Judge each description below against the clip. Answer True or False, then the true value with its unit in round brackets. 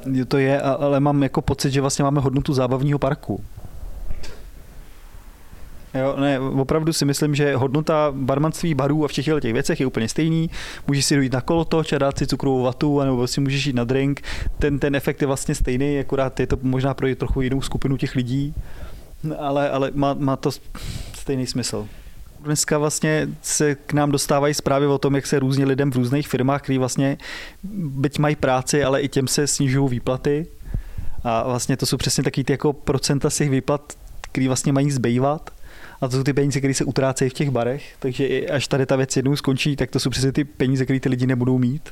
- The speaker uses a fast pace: True (200 wpm)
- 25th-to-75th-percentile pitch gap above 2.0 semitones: False (1.7 semitones)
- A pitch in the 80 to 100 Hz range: False (140 Hz)